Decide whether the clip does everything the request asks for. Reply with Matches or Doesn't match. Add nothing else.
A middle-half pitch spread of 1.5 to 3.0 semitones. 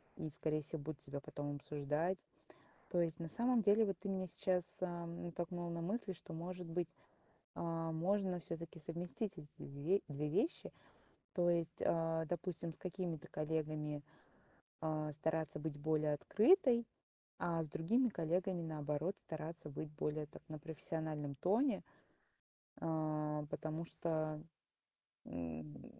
Matches